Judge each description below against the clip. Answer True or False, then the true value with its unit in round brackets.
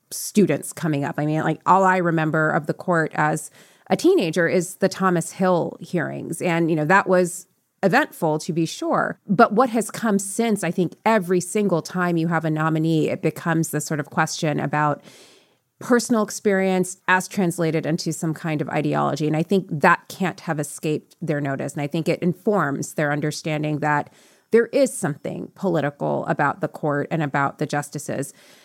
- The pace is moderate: True (180 wpm)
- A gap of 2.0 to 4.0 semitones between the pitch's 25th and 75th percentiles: True (3.4 semitones)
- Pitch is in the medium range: True (165 Hz)